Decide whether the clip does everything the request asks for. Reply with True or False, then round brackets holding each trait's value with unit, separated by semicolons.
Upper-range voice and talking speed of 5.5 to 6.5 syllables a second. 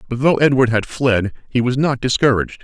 False (125 Hz; 5.7 syllables/s)